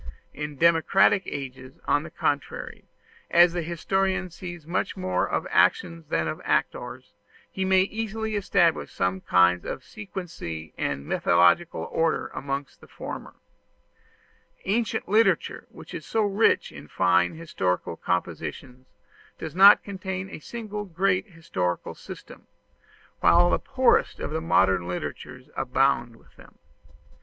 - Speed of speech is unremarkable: No, slow, 130 wpm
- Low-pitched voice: No, medium, 165 Hz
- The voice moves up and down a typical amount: No, wide, 7.5 semitones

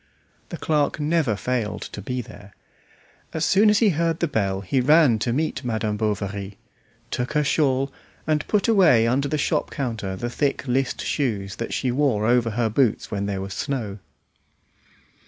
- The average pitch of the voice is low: Yes, low, 125 Hz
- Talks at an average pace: Yes, average, 175 wpm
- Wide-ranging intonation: Yes, wide, 6.0 semitones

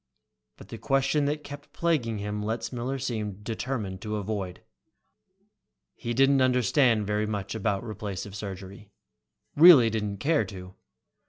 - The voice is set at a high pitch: No, low, 110 Hz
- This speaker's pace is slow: Yes, slow, 130 wpm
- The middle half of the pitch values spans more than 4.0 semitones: Yes, average, 4.7 semitones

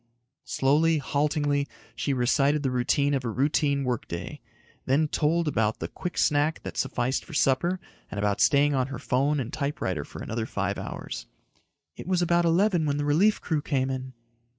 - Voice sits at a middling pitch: Yes, medium, 145 Hz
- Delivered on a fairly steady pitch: No, average, 3.1 semitones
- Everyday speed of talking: Yes, average, 175 wpm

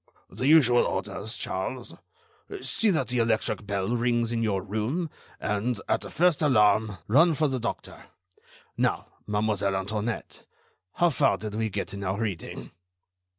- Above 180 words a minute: No, average, 150 wpm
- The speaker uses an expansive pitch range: No, average, 3.7 semitones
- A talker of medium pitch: No, low, 110 Hz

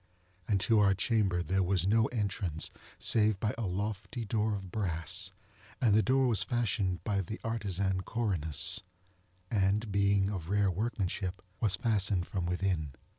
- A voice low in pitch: Yes, low, 100 Hz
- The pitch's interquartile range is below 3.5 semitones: Yes, average, 2.8 semitones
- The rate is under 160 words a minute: Yes, average, 150 wpm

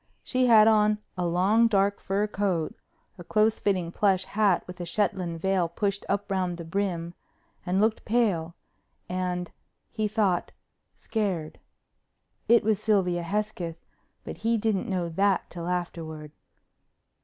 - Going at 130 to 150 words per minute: Yes, average, 140 wpm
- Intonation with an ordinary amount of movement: Yes, average, 3.3 semitones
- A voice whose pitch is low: No, high, 190 Hz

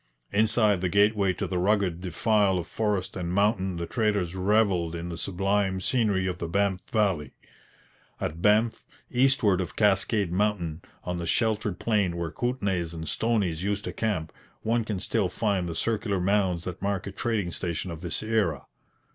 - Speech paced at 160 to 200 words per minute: Yes, average, 170 wpm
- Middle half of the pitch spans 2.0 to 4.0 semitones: Yes, average, 3.3 semitones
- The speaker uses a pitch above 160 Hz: No, very low, 95 Hz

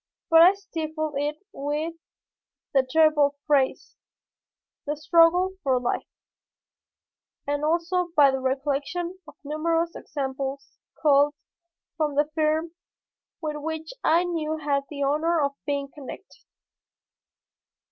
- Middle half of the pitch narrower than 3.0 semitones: Yes, narrow, 2.6 semitones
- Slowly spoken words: Yes, slow, 115 wpm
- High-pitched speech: Yes, very high, 300 Hz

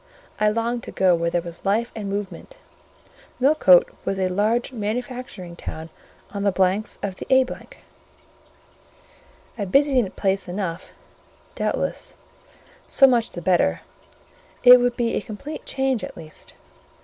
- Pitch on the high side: Yes, high, 205 Hz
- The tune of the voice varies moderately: Yes, average, 4.9 semitones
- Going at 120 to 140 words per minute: Yes, slow, 135 wpm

